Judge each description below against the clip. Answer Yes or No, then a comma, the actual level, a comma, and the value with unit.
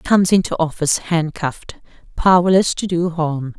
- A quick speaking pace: No, average, 150 wpm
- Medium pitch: Yes, medium, 170 Hz